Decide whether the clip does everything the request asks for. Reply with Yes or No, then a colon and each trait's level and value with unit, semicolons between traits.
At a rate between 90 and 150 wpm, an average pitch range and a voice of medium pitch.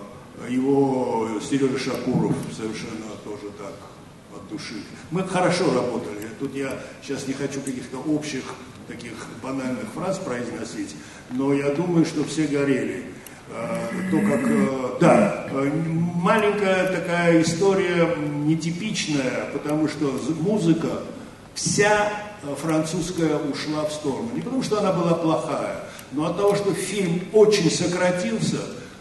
Yes: average, 115 wpm; average, 4.8 semitones; medium, 155 Hz